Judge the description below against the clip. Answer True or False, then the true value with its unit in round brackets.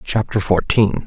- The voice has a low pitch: True (105 Hz)